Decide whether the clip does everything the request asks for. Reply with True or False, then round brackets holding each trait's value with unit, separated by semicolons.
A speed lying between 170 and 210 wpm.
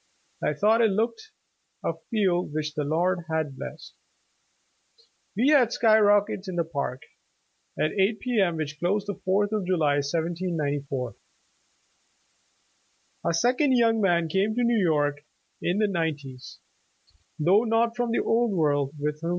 False (150 wpm)